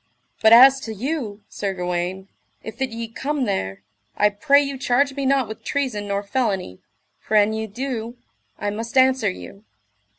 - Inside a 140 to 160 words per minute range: No, average, 170 wpm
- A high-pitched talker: Yes, high, 225 Hz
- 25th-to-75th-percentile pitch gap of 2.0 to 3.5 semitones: No, average, 4.5 semitones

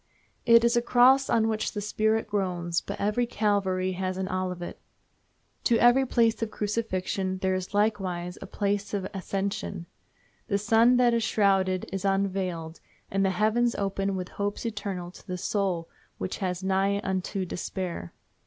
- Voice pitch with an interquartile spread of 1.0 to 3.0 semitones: Yes, average, 2.7 semitones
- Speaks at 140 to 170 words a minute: Yes, average, 160 wpm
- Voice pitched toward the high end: Yes, high, 195 Hz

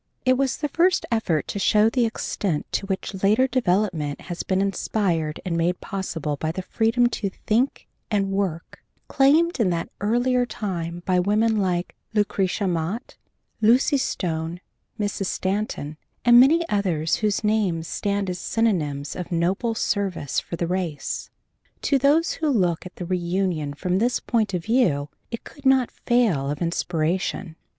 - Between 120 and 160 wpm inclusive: Yes, average, 155 wpm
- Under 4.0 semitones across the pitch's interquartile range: No, average, 5.0 semitones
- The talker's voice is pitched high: Yes, high, 195 Hz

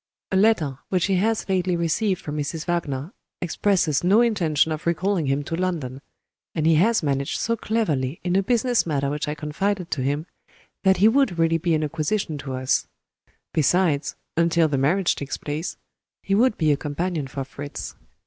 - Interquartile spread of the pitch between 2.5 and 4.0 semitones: No, average, 4.6 semitones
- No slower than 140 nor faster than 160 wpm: No, average, 180 wpm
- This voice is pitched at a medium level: Yes, medium, 165 Hz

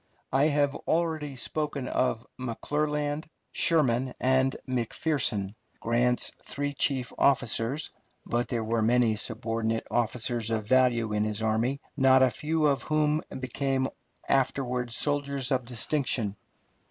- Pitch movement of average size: Yes, average, 3.6 semitones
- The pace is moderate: No, slow, 120 wpm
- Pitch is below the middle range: Yes, low, 130 Hz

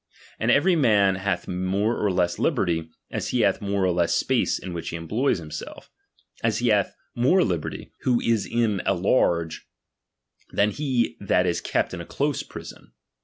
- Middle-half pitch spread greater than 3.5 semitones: Yes, average, 4.9 semitones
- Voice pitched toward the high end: No, low, 100 Hz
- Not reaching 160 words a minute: No, average, 175 wpm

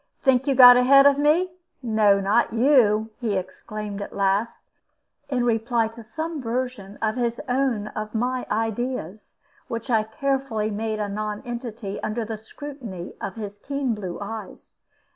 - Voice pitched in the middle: No, high, 225 Hz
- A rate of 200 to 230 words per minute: No, average, 150 wpm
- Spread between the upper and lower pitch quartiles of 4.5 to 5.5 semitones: No, average, 3.2 semitones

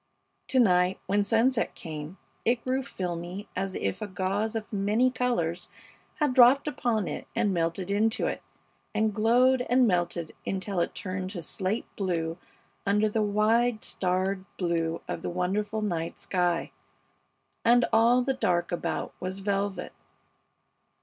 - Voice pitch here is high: Yes, high, 200 Hz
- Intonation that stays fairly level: No, average, 4.1 semitones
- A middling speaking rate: Yes, average, 145 wpm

